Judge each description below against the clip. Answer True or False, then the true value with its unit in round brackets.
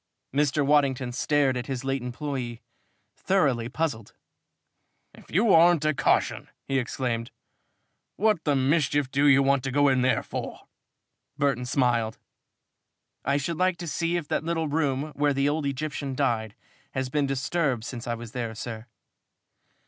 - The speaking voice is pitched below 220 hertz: True (140 Hz)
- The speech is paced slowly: False (155 wpm)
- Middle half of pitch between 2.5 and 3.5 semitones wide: True (3.2 semitones)